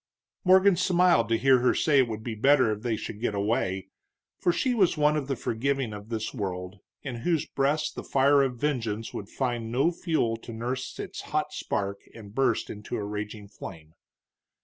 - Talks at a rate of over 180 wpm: Yes, average, 190 wpm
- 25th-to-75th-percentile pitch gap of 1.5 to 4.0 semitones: No, average, 4.9 semitones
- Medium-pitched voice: No, low, 120 Hz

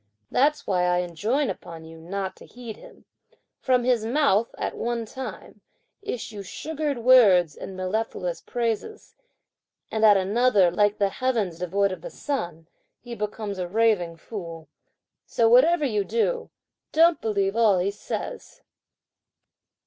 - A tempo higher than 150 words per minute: No, average, 140 wpm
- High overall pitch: Yes, high, 215 Hz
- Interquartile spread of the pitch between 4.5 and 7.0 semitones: Yes, average, 5.1 semitones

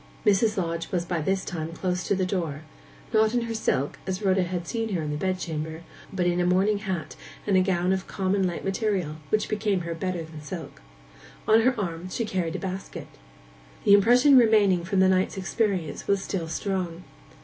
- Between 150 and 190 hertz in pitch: Yes, medium, 185 Hz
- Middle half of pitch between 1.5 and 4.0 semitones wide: Yes, average, 2.9 semitones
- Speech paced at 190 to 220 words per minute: Yes, average, 195 wpm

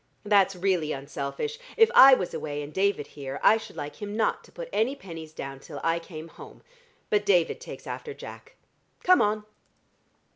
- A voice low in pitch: No, high, 190 Hz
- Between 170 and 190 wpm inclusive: Yes, average, 180 wpm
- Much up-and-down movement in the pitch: Yes, wide, 6.0 semitones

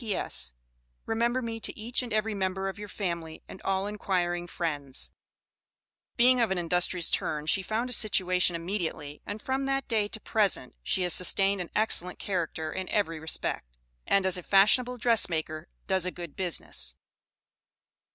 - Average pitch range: Yes, average, 4.1 semitones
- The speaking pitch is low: No, high, 190 Hz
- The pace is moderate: Yes, average, 165 wpm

